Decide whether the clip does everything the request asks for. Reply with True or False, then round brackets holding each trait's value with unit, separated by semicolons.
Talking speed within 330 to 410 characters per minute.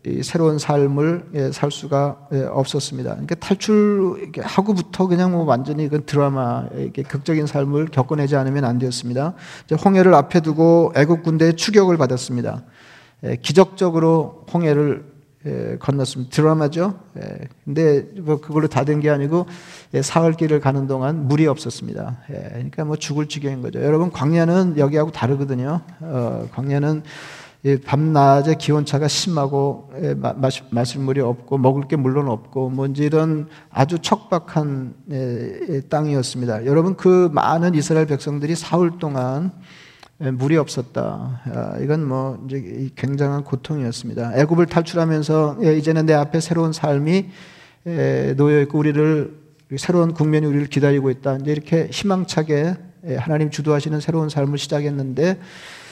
True (335 characters per minute)